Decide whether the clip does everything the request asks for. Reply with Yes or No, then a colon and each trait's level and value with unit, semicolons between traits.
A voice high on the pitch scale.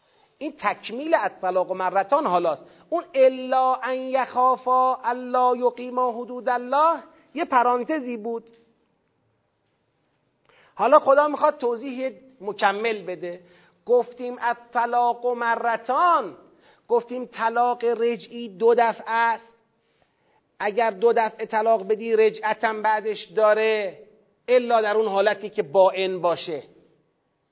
Yes: high, 235 Hz